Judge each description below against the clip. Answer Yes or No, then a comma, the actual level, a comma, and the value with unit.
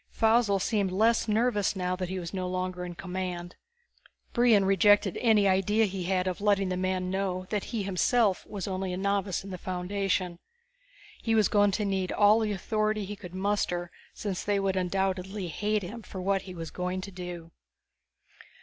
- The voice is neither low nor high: No, high, 195 Hz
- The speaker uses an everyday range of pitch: No, narrow, 2.1 semitones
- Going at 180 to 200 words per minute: Yes, average, 185 wpm